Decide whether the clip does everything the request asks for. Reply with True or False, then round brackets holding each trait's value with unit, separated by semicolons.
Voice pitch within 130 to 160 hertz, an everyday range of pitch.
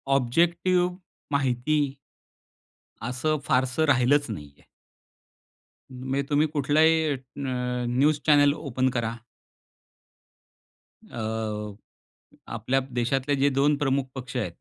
True (135 Hz; 3.2 semitones)